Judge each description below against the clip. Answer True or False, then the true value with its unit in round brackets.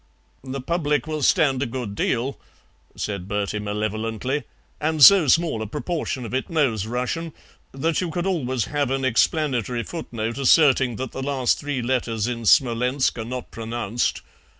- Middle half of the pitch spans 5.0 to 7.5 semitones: False (4.3 semitones)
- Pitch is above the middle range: False (130 Hz)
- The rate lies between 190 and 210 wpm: False (155 wpm)